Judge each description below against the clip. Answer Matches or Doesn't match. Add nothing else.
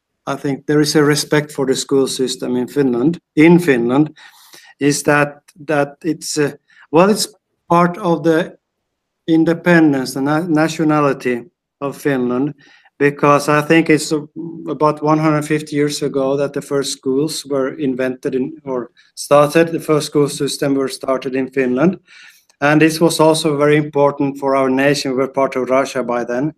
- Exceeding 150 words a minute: Matches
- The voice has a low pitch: Doesn't match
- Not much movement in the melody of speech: Matches